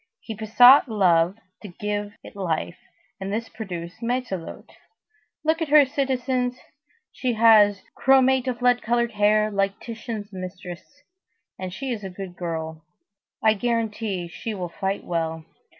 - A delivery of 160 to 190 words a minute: No, average, 145 wpm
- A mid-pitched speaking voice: No, high, 210 Hz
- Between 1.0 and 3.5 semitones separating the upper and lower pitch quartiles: No, average, 4.7 semitones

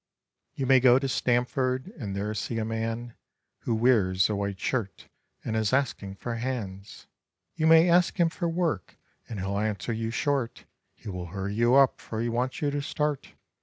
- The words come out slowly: No, average, 185 wpm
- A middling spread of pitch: Yes, average, 4.4 semitones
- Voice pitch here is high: No, low, 120 Hz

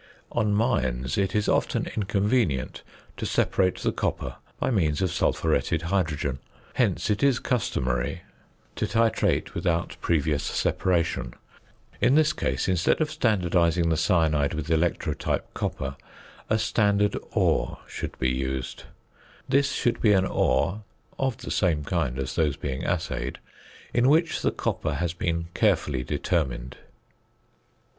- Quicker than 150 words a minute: No, slow, 135 wpm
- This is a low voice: Yes, very low, 85 Hz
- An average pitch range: No, wide, 6.4 semitones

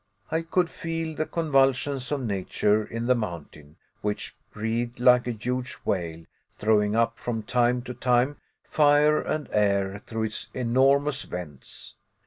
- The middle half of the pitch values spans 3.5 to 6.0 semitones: Yes, average, 4.8 semitones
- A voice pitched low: Yes, low, 120 Hz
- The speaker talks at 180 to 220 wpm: No, average, 140 wpm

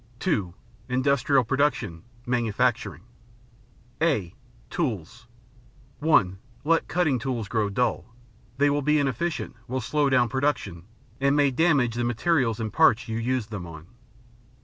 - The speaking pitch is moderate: No, low, 125 Hz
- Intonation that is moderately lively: Yes, average, 4.6 semitones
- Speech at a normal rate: No, slow, 125 wpm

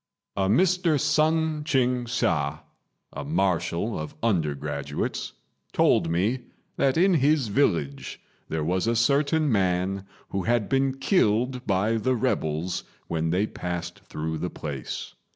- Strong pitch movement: Yes, wide, 7.9 semitones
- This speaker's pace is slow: Yes, slow, 130 wpm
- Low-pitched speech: Yes, low, 105 Hz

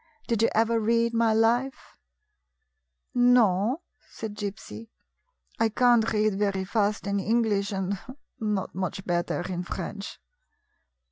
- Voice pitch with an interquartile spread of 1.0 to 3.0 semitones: Yes, narrow, 2.6 semitones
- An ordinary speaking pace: No, slow, 125 wpm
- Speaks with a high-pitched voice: Yes, high, 215 Hz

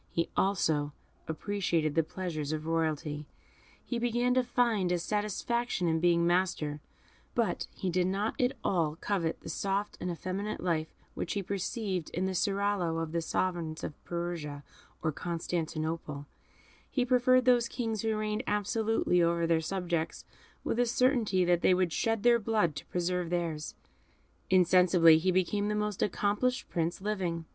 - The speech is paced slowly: No, average, 155 wpm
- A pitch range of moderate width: Yes, average, 4.2 semitones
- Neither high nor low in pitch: Yes, medium, 180 Hz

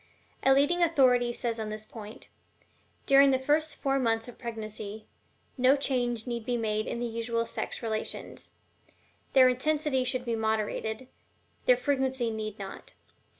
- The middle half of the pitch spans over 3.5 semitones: No, average, 3.2 semitones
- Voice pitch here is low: No, high, 240 Hz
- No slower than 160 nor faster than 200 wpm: No, average, 150 wpm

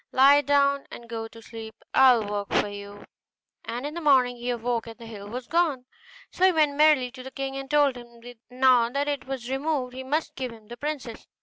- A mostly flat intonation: No, average, 3.3 semitones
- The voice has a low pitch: No, very high, 255 Hz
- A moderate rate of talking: No, fast, 230 wpm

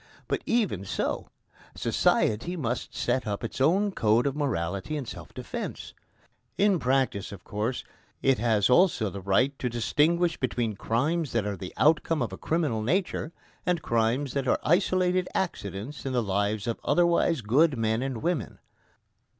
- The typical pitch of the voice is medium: No, low, 125 Hz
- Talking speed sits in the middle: Yes, average, 160 wpm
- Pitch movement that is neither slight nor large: No, wide, 7.0 semitones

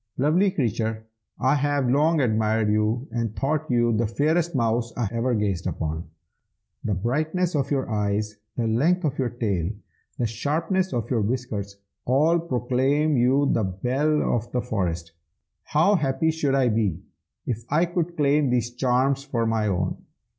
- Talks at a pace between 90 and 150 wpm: No, average, 160 wpm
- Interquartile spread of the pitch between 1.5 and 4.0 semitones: No, average, 4.9 semitones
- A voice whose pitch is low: Yes, low, 125 Hz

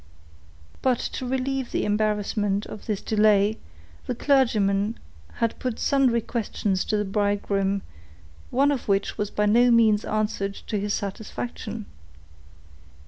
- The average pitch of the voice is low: No, high, 215 Hz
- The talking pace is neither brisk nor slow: No, slow, 130 wpm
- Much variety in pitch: No, average, 2.7 semitones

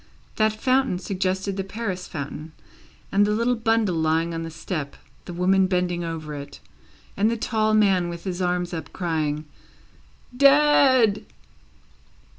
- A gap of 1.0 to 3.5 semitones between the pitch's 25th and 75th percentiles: No, average, 4.5 semitones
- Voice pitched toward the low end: No, medium, 185 Hz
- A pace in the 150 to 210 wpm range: No, slow, 135 wpm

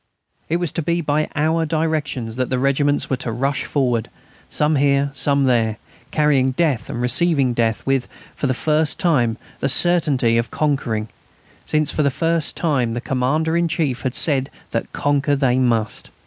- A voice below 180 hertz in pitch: Yes, medium, 140 Hz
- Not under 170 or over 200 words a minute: Yes, average, 175 wpm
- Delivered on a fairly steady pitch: No, average, 3.6 semitones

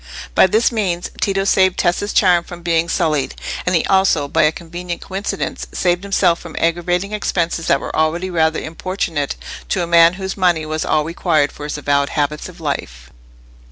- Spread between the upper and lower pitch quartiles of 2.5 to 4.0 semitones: Yes, average, 2.9 semitones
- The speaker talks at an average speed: Yes, average, 180 wpm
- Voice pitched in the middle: Yes, medium, 170 Hz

